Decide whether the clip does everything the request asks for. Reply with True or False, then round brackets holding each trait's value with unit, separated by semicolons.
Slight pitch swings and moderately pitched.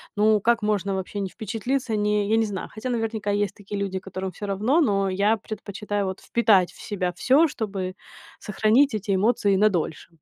False (2.2 semitones; 205 Hz)